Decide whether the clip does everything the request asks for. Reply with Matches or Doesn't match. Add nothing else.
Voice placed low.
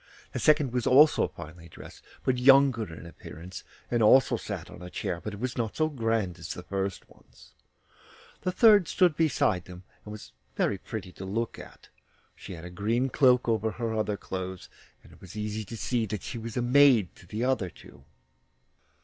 Matches